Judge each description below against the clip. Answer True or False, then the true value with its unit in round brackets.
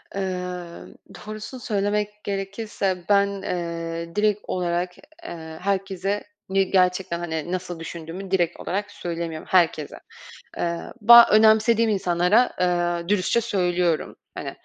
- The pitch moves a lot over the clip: False (3.0 semitones)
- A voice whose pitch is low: False (185 Hz)